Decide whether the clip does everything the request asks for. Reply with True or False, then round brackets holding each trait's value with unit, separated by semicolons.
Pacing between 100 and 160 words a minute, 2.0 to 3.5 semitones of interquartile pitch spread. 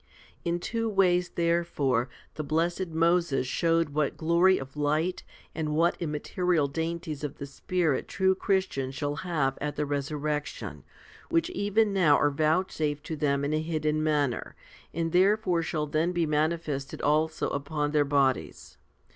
True (150 wpm; 3.0 semitones)